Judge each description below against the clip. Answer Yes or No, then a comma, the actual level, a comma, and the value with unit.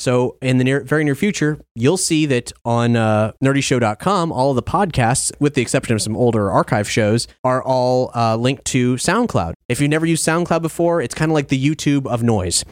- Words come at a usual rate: No, fast, 210 wpm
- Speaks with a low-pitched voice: Yes, low, 130 Hz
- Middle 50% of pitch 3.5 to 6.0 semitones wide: Yes, average, 4.2 semitones